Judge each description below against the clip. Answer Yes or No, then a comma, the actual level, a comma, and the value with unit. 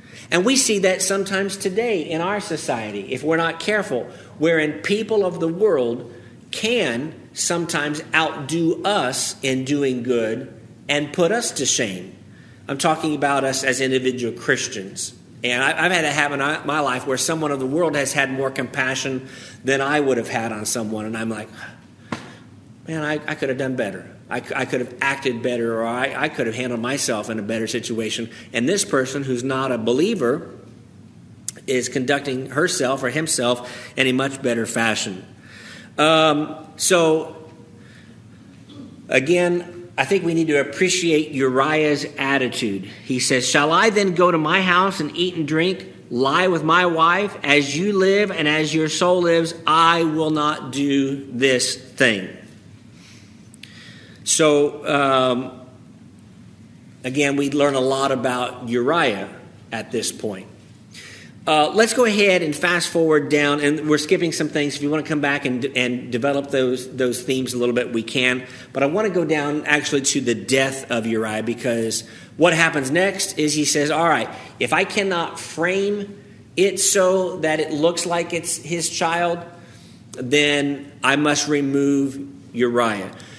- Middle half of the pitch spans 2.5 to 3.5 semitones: No, average, 4.6 semitones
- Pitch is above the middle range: No, medium, 140 Hz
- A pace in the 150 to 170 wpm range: Yes, average, 165 wpm